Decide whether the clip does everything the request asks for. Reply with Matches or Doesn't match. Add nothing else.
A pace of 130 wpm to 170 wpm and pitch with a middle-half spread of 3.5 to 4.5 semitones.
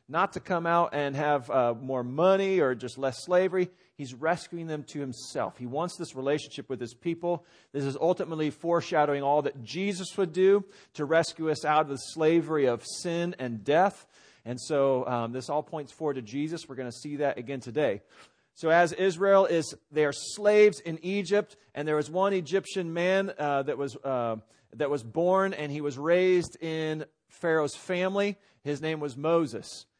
Doesn't match